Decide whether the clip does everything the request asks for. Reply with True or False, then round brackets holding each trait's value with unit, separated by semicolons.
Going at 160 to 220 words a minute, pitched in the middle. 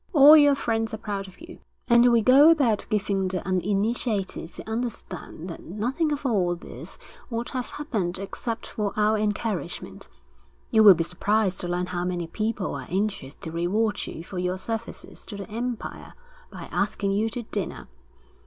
False (170 wpm; 210 Hz)